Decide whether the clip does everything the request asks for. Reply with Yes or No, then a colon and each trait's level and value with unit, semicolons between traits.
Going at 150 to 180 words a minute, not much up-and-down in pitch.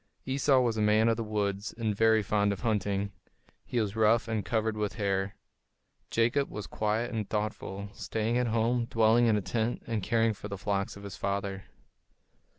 No: average, 190 wpm; narrow, 2.2 semitones